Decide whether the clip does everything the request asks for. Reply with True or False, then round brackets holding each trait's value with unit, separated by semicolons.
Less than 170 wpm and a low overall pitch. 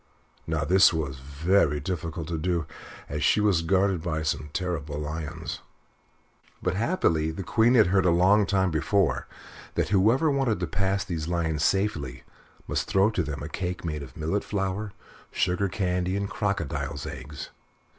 True (160 wpm; 90 Hz)